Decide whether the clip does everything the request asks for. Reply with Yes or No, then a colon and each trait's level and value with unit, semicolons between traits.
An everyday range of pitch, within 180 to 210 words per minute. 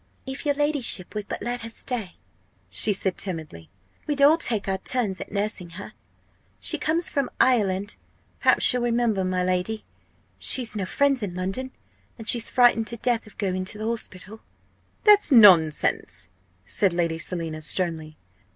No: average, 5.0 semitones; average, 160 wpm